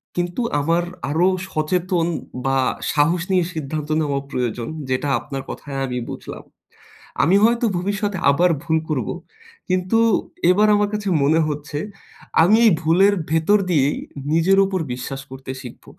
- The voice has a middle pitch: Yes, medium, 165 Hz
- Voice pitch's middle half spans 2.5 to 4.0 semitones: No, average, 4.6 semitones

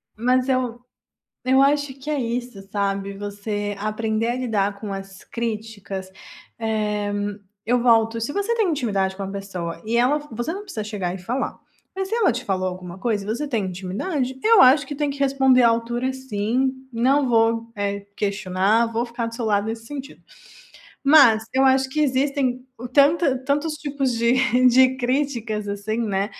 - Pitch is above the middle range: Yes, high, 235 Hz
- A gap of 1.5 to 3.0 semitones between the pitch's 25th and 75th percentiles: No, average, 4.5 semitones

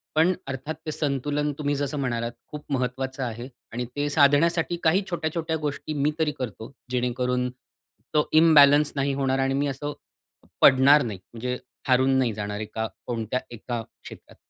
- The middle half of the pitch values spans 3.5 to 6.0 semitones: No, average, 2.9 semitones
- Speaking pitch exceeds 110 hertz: Yes, low, 135 Hz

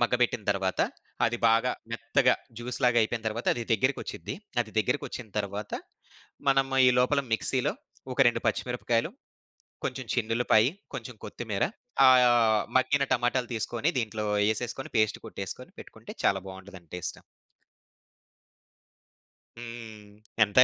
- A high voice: No, low, 120 Hz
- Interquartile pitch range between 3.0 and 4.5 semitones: No, narrow, 2.5 semitones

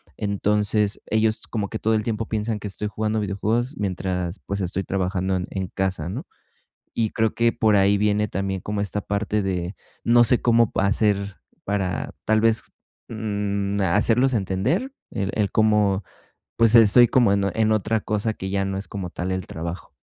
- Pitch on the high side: No, low, 105 Hz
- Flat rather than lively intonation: Yes, narrow, 2.1 semitones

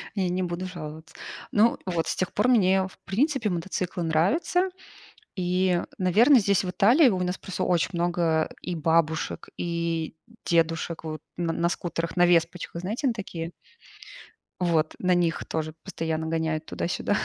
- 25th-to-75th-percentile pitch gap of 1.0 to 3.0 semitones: Yes, narrow, 2.5 semitones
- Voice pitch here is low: No, medium, 175 Hz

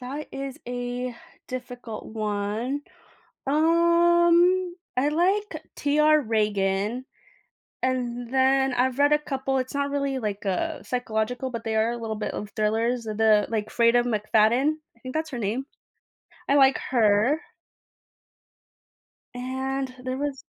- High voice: Yes, very high, 255 Hz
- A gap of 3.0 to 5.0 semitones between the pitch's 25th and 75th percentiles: Yes, average, 4.1 semitones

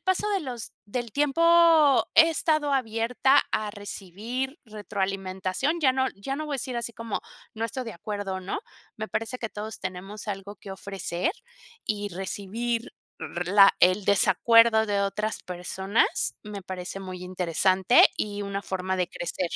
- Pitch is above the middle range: Yes, high, 210 Hz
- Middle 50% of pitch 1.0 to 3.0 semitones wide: No, average, 4.6 semitones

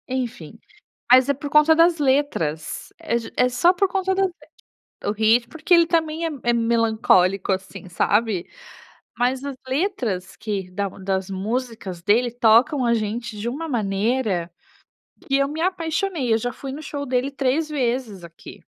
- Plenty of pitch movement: Yes, wide, 5.8 semitones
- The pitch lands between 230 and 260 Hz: Yes, high, 245 Hz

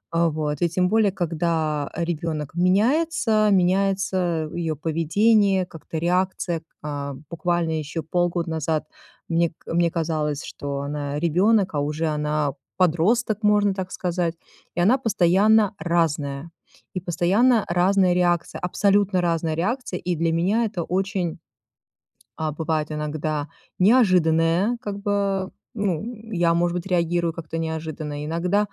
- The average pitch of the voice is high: No, medium, 175 Hz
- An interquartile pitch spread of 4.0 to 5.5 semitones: No, average, 3.3 semitones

